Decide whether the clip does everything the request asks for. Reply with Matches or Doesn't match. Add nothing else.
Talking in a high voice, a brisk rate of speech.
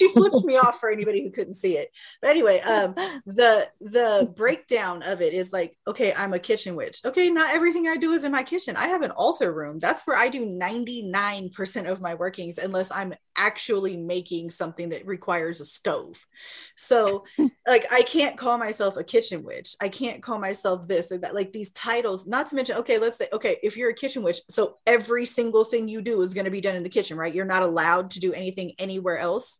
Matches